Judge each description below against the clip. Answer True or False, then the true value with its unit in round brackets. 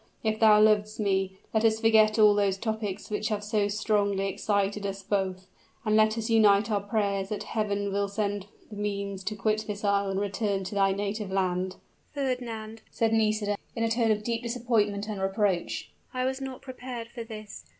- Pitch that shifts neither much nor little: False (1.7 semitones)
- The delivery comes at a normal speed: True (190 wpm)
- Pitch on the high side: True (210 Hz)